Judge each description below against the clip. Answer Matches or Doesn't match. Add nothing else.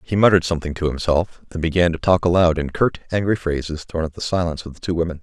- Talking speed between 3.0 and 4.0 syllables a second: Doesn't match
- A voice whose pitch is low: Matches